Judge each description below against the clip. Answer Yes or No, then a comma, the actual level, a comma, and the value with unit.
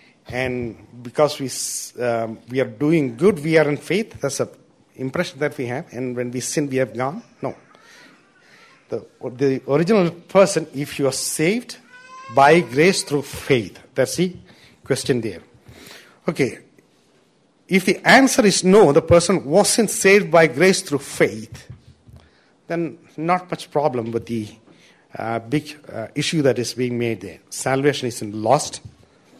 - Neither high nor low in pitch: Yes, medium, 145 Hz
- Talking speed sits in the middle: Yes, average, 150 wpm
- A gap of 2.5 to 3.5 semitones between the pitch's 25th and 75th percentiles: No, wide, 5.4 semitones